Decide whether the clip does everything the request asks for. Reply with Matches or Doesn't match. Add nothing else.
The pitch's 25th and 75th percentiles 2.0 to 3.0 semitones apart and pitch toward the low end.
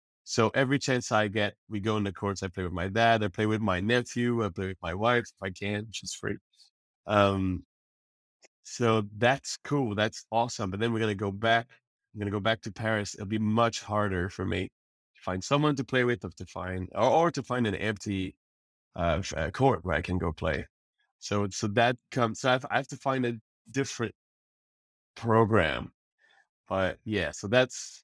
Doesn't match